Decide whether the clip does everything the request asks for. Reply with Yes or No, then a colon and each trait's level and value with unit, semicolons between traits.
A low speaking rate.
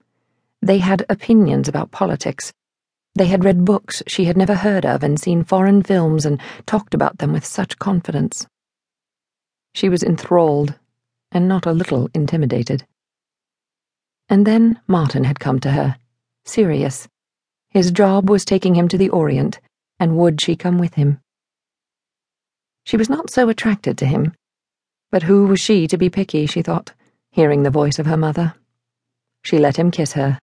No: average, 160 wpm